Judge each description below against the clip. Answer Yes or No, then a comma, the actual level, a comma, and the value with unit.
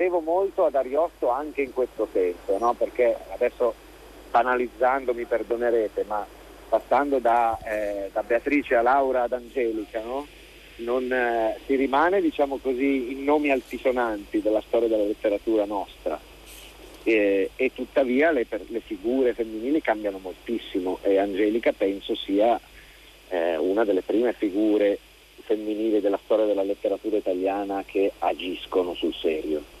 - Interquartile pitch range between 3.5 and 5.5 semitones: Yes, average, 4.4 semitones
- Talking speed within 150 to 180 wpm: No, average, 130 wpm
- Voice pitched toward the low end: Yes, low, 115 Hz